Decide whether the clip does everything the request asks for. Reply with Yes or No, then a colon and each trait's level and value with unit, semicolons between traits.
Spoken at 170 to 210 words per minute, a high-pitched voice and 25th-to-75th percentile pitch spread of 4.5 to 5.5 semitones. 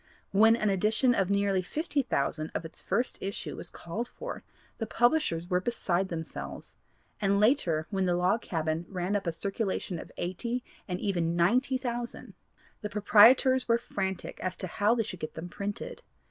Yes: average, 175 wpm; high, 200 Hz; average, 4.8 semitones